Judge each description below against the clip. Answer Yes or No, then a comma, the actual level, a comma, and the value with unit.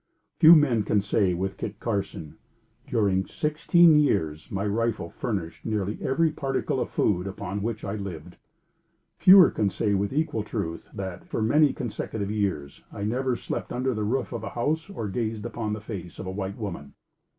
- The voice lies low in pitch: Yes, low, 105 Hz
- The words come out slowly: No, average, 175 wpm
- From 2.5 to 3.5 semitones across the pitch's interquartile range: No, average, 4.2 semitones